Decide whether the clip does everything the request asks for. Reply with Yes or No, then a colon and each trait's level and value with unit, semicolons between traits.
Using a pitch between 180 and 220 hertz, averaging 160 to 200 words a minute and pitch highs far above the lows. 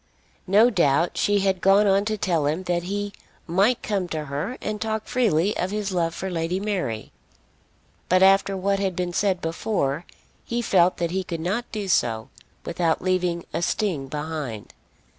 No: medium, 185 Hz; average, 175 wpm; average, 3.4 semitones